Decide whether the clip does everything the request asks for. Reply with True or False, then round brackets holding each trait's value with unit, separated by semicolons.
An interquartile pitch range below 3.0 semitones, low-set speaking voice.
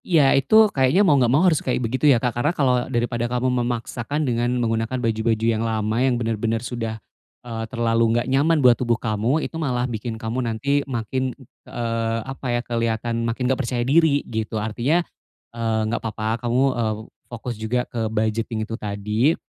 True (2.5 semitones; 120 Hz)